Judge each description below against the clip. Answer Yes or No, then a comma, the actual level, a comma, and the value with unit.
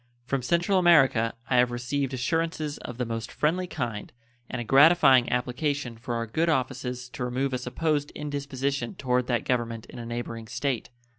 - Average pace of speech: Yes, average, 170 wpm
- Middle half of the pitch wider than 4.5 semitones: No, average, 3.0 semitones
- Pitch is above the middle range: No, low, 130 Hz